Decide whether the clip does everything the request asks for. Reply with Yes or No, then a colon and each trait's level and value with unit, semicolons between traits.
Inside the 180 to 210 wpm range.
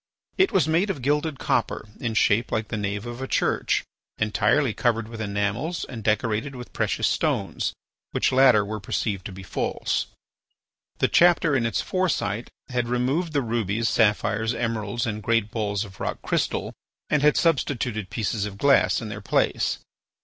No: average, 165 wpm